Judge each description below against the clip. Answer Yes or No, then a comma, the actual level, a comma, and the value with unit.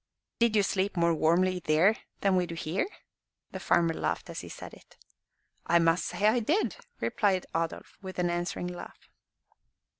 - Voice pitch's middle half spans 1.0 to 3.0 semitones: Yes, average, 2.7 semitones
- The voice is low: No, medium, 180 Hz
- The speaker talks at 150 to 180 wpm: Yes, average, 160 wpm